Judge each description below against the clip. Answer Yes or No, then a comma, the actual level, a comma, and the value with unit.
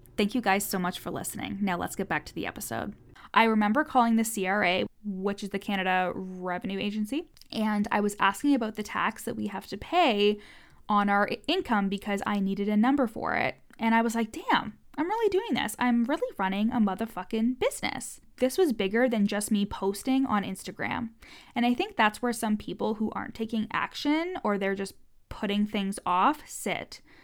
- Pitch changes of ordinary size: Yes, average, 3.6 semitones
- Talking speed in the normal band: Yes, average, 195 wpm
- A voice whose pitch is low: No, high, 215 Hz